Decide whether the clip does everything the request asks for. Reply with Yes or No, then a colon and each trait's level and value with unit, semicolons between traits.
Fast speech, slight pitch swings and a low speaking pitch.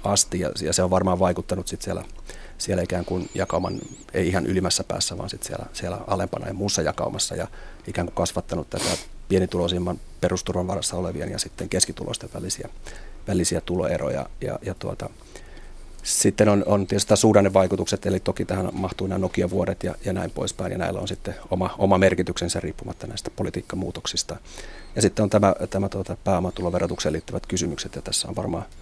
Yes: fast, 170 wpm; narrow, 1.8 semitones; very low, 95 Hz